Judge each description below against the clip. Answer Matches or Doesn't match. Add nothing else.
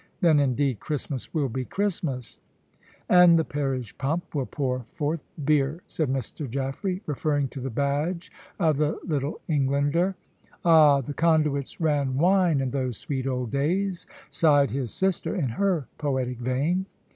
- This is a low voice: Doesn't match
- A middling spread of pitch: Matches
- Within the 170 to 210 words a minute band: Doesn't match